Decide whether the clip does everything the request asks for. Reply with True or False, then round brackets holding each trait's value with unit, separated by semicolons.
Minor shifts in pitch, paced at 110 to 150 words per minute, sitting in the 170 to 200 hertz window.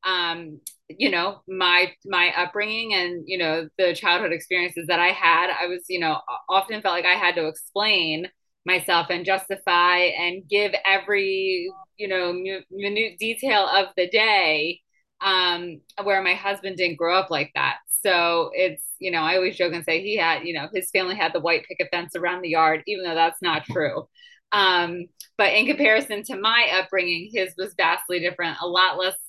False (2.3 semitones; 185 wpm; 185 Hz)